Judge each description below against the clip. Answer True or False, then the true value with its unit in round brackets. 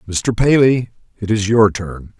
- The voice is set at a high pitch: False (110 Hz)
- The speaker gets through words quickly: False (165 wpm)